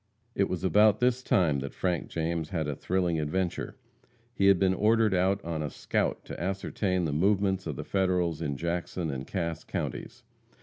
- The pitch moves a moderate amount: Yes, average, 3.2 semitones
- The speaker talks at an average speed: Yes, average, 180 wpm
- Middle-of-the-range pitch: No, very low, 90 Hz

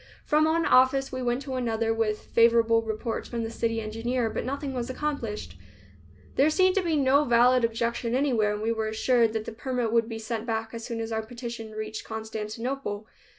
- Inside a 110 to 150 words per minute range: No, average, 195 wpm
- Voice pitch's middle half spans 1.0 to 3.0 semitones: Yes, narrow, 2.5 semitones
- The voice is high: Yes, high, 230 Hz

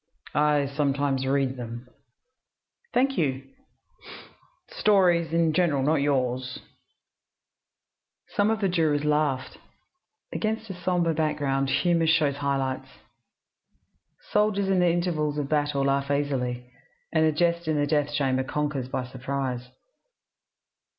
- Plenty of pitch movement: No, average, 3.8 semitones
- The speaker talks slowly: Yes, slow, 120 wpm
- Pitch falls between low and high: Yes, medium, 145 Hz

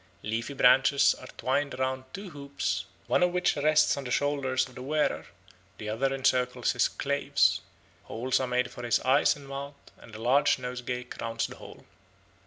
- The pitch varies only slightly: Yes, narrow, 2.2 semitones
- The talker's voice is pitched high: No, low, 130 Hz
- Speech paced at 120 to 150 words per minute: No, average, 180 wpm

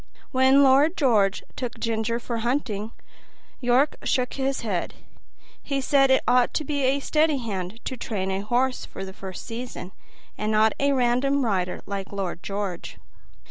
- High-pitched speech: Yes, high, 240 Hz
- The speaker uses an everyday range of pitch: Yes, average, 4.9 semitones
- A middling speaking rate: Yes, average, 160 wpm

